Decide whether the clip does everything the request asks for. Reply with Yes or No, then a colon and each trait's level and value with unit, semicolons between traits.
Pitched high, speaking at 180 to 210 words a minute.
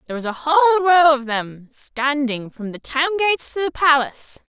Yes: very high, 285 Hz; average, 200 wpm